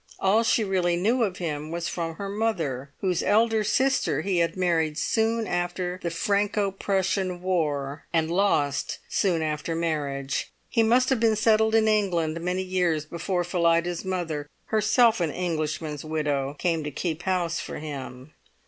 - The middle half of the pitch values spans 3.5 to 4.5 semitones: Yes, average, 4.2 semitones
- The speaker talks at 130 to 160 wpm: Yes, average, 155 wpm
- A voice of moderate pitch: Yes, medium, 175 Hz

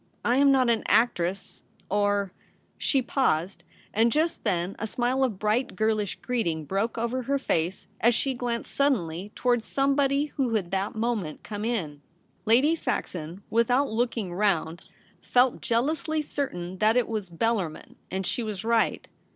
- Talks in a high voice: Yes, high, 225 Hz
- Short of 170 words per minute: Yes, average, 160 wpm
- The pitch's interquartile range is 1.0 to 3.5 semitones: No, average, 4.7 semitones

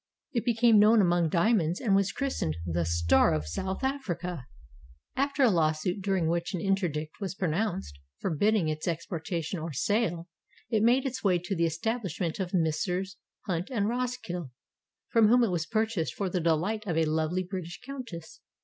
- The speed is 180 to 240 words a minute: No, average, 170 wpm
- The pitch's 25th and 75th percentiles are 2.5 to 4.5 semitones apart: No, average, 5.0 semitones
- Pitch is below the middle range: No, medium, 185 Hz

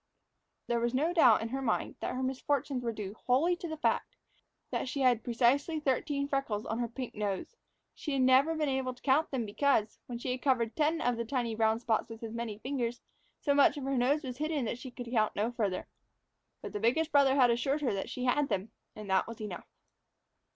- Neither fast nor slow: No, fast, 225 wpm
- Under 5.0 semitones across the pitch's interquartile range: Yes, average, 3.5 semitones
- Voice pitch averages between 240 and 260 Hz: Yes, very high, 250 Hz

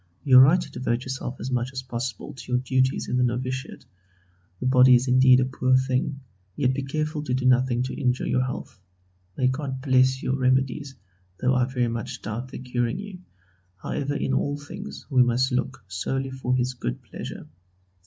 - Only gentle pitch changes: Yes, narrow, 1.0 semitones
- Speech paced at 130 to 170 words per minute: No, average, 195 wpm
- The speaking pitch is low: Yes, low, 130 Hz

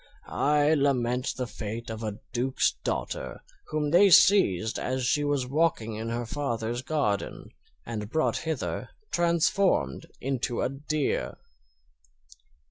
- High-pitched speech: No, low, 130 Hz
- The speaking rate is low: Yes, slow, 125 wpm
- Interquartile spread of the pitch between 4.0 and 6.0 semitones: Yes, average, 4.7 semitones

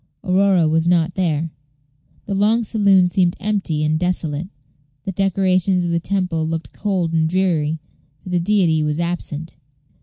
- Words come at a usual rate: Yes, average, 150 wpm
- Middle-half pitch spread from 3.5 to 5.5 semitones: No, average, 3.0 semitones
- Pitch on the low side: No, medium, 175 Hz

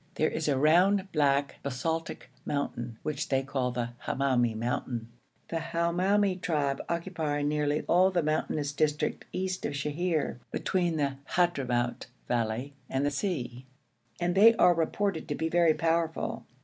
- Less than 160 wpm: Yes, average, 145 wpm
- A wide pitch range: No, average, 4.1 semitones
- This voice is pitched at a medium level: Yes, medium, 150 Hz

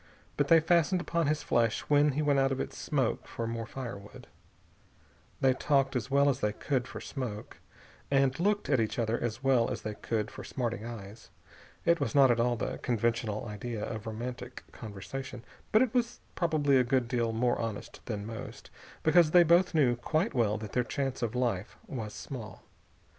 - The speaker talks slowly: No, average, 190 wpm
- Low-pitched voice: Yes, low, 125 Hz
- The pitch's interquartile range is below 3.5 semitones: No, average, 3.9 semitones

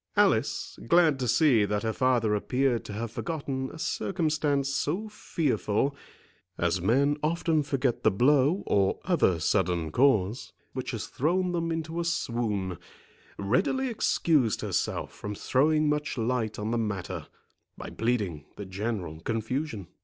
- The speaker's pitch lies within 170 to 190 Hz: No, low, 125 Hz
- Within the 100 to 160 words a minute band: Yes, average, 140 wpm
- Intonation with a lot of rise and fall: Yes, wide, 6.6 semitones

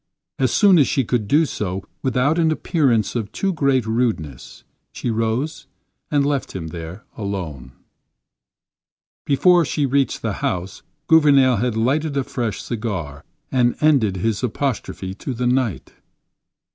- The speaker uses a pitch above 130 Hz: No, low, 125 Hz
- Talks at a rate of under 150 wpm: Yes, average, 140 wpm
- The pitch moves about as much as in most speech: No, wide, 5.7 semitones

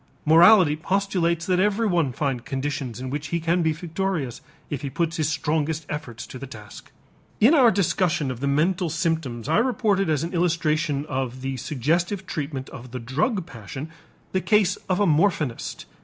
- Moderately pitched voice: Yes, medium, 160 Hz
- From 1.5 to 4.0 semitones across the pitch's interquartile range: No, average, 4.7 semitones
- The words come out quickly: No, average, 170 wpm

